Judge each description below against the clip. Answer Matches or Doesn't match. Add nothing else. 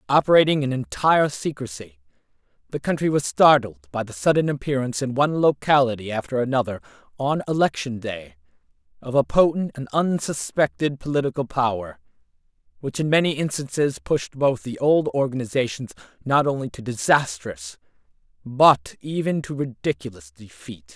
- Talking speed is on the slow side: Matches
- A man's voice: Matches